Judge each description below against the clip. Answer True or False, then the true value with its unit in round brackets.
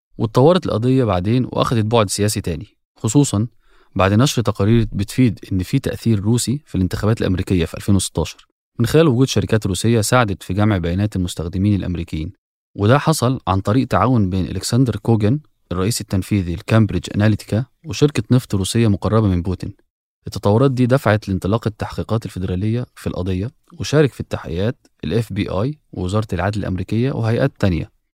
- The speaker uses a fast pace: True (145 wpm)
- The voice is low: True (105 Hz)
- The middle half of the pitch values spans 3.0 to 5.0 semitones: True (3.8 semitones)